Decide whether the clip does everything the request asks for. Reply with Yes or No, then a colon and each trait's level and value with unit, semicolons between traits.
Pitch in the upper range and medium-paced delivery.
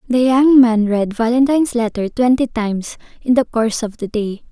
Yes: high, 235 Hz; average, 185 wpm